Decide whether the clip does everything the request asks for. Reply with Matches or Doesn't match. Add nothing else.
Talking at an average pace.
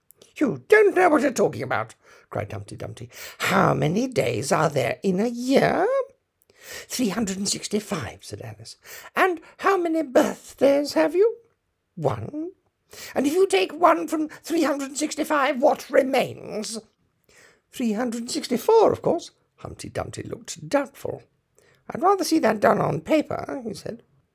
Matches